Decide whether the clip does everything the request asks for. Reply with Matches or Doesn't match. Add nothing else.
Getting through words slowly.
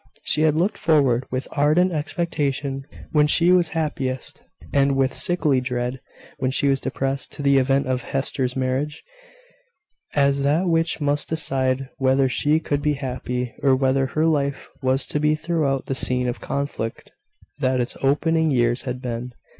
Doesn't match